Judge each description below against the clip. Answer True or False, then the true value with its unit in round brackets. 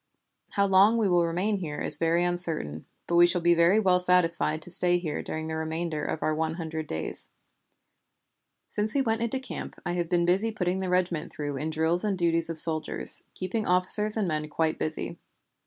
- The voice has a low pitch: False (175 Hz)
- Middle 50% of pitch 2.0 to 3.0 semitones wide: True (2.6 semitones)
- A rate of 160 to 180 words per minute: False (195 wpm)